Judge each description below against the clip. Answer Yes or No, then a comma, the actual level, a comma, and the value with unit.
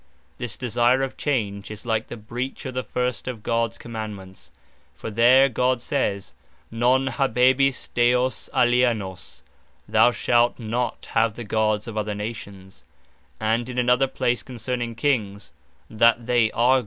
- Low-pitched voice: Yes, low, 120 Hz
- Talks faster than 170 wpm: No, average, 145 wpm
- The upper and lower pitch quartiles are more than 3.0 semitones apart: No, narrow, 2.5 semitones